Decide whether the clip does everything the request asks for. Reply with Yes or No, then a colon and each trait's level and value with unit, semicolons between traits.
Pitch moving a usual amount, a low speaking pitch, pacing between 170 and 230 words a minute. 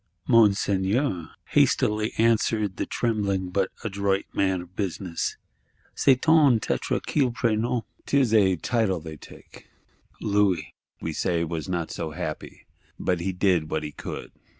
No: average, 4.0 semitones; low, 100 Hz; slow, 135 wpm